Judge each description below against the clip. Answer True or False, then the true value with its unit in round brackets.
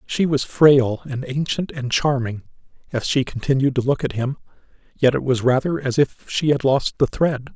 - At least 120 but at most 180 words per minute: False (200 wpm)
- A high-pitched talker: False (135 Hz)